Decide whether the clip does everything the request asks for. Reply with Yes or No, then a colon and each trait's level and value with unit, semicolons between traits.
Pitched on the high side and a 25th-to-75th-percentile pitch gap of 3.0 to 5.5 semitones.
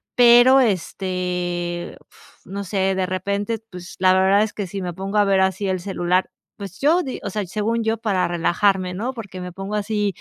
No: high, 195 Hz; narrow, 2.4 semitones